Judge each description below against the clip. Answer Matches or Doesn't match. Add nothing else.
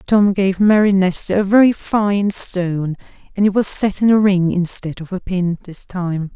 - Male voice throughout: Doesn't match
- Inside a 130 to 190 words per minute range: Doesn't match